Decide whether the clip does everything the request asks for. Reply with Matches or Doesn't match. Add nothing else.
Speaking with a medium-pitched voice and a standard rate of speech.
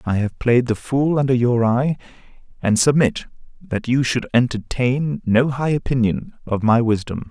Doesn't match